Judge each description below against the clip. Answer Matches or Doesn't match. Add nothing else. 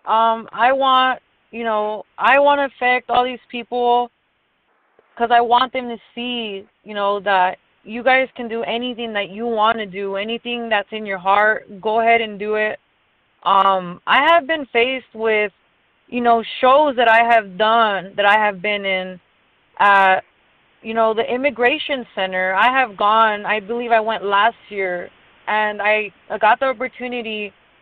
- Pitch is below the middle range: Doesn't match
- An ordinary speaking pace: Matches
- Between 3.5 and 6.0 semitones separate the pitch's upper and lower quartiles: Doesn't match